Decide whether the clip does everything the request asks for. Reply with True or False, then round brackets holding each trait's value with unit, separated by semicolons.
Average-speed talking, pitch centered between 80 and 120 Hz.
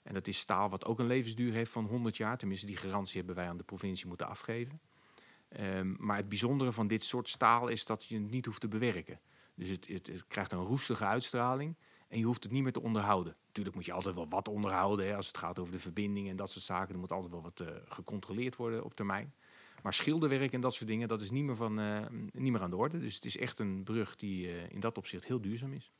False (260 wpm; 105 Hz)